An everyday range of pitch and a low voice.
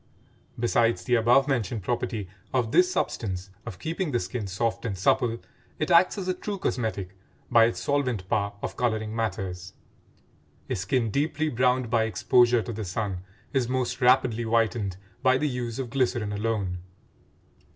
Yes: average, 3.8 semitones; low, 115 Hz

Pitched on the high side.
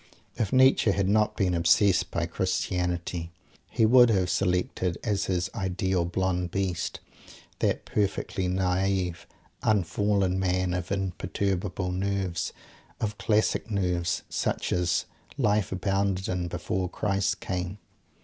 No: very low, 95 Hz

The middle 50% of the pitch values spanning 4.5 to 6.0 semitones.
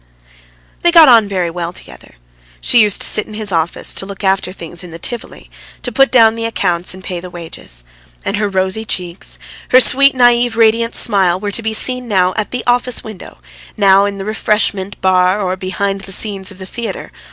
No: average, 3.7 semitones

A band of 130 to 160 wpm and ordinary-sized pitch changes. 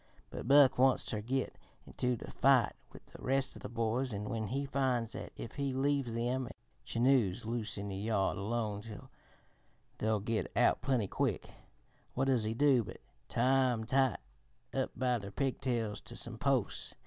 No: average, 170 wpm; average, 3.3 semitones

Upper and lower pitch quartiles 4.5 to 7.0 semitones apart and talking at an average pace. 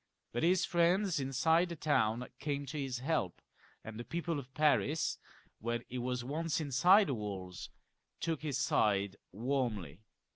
Yes: wide, 5.6 semitones; average, 150 wpm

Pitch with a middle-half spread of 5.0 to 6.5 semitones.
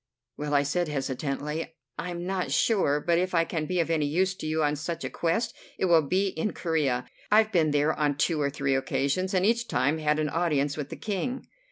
No: average, 3.8 semitones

